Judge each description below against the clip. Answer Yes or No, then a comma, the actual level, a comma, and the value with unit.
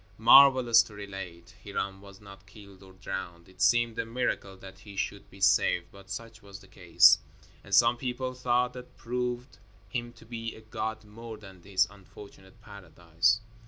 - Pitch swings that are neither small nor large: Yes, average, 3.5 semitones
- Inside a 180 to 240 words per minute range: No, average, 170 wpm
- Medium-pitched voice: No, low, 105 Hz